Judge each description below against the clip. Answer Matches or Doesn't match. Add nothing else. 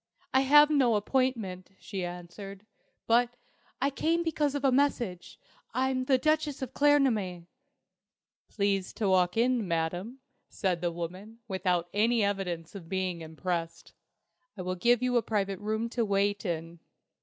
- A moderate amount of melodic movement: Doesn't match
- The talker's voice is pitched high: Matches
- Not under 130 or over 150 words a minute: Matches